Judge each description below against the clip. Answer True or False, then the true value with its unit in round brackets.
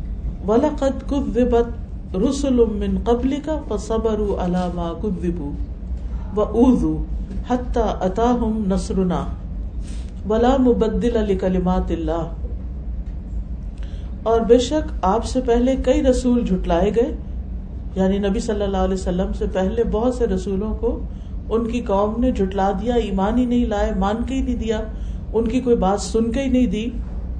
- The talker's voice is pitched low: False (215 Hz)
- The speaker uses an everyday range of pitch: True (4.4 semitones)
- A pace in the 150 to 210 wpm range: False (140 wpm)